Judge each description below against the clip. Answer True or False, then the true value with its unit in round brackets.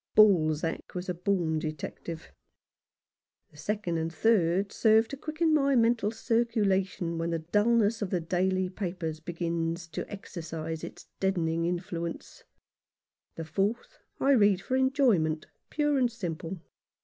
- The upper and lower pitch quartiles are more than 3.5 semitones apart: True (5.2 semitones)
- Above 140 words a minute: False (135 wpm)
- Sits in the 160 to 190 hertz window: True (185 Hz)